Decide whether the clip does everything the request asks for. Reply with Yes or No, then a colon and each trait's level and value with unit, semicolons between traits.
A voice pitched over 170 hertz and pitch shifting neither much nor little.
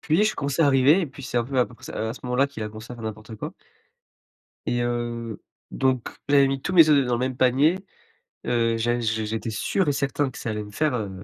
No: low, 125 Hz; average, 3.6 semitones